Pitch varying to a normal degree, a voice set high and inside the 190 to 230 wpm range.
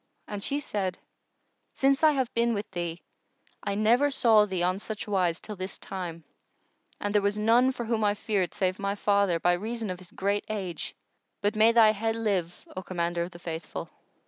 Yes: average, 3.4 semitones; high, 205 Hz; average, 195 wpm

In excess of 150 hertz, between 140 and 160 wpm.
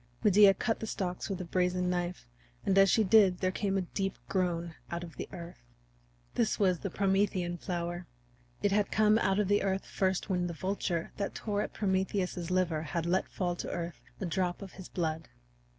No: medium, 185 Hz; average, 200 wpm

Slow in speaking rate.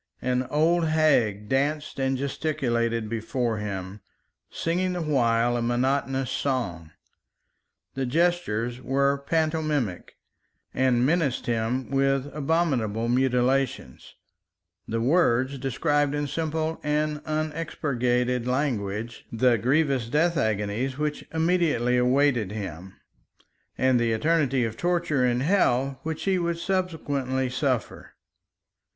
Yes: slow, 110 wpm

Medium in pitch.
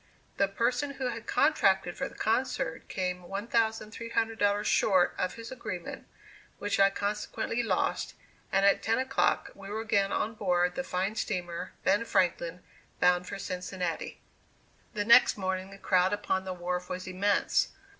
No: high, 195 Hz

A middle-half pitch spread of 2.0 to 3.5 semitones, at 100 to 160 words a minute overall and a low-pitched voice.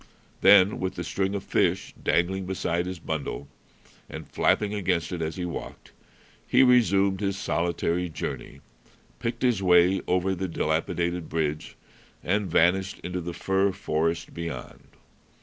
Yes: narrow, 2.4 semitones; average, 140 wpm; very low, 90 Hz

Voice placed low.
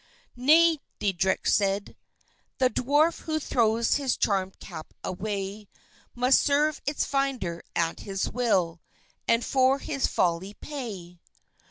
No: high, 230 Hz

